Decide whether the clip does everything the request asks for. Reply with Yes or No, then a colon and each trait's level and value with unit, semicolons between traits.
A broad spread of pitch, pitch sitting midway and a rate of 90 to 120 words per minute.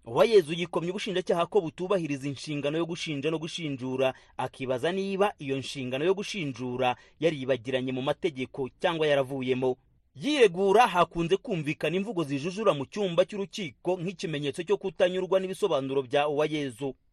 No: wide, 5.8 semitones; medium, 165 Hz; average, 130 wpm